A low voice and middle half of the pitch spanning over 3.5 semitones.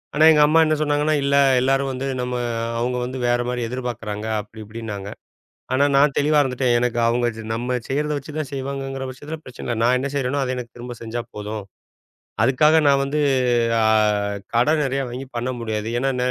No: low, 130 Hz; average, 2.8 semitones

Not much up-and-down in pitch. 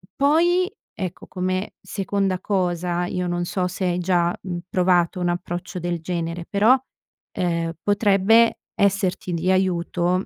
Yes: narrow, 2.0 semitones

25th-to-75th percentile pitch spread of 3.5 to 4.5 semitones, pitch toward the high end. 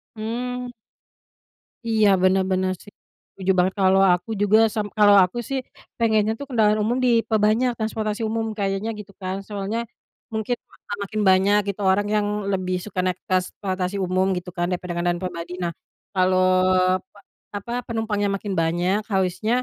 No: average, 2.7 semitones; high, 205 Hz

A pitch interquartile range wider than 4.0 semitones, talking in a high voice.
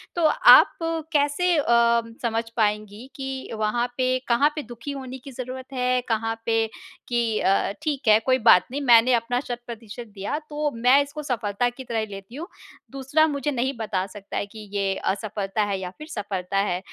Yes: average, 4.5 semitones; high, 240 Hz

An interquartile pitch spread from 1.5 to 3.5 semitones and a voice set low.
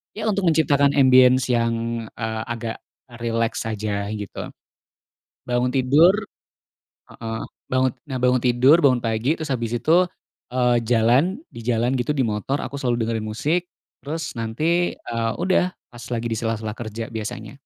Yes: average, 2.8 semitones; low, 120 Hz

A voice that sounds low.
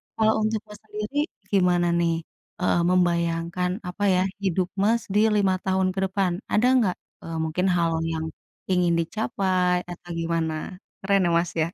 No: medium, 180 Hz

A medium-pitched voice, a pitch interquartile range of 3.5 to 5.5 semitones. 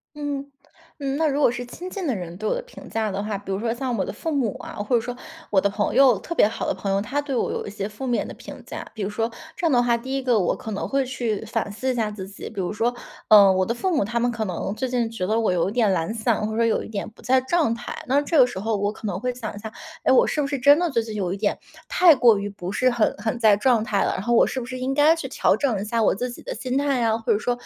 No: high, 230 Hz; average, 4.0 semitones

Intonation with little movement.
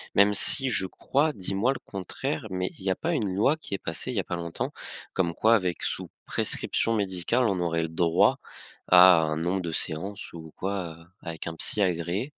No: average, 3.5 semitones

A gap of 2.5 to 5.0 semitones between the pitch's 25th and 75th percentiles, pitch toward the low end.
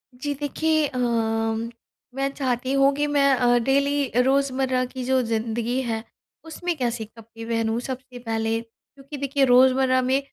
No: average, 3.0 semitones; very high, 255 Hz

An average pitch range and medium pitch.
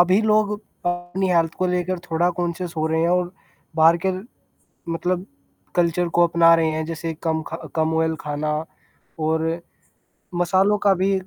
No: narrow, 2.0 semitones; medium, 170 Hz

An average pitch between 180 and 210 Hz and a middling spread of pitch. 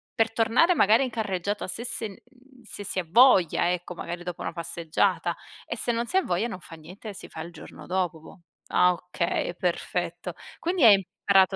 Yes: high, 190 Hz; average, 4.8 semitones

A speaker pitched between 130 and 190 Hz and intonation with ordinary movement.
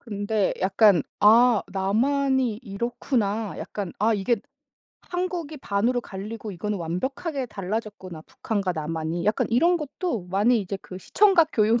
No: high, 215 Hz; average, 4.4 semitones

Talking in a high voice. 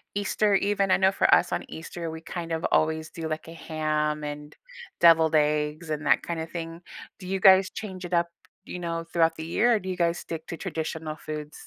No: medium, 165 Hz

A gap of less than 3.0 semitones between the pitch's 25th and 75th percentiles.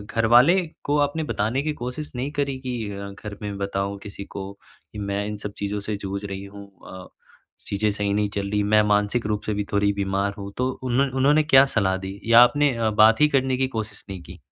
No: average, 4.2 semitones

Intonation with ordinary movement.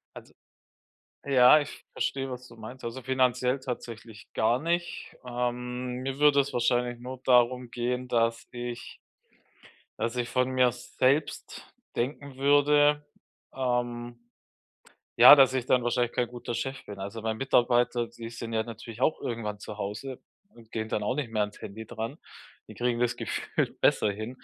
No: narrow, 2.0 semitones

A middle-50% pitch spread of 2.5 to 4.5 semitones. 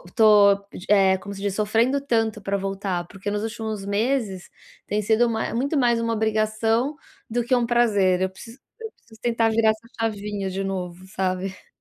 Yes: average, 2.8 semitones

